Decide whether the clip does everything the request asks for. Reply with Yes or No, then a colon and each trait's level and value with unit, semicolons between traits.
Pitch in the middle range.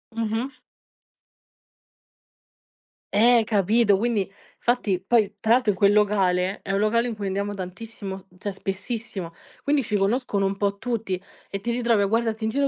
No: high, 210 Hz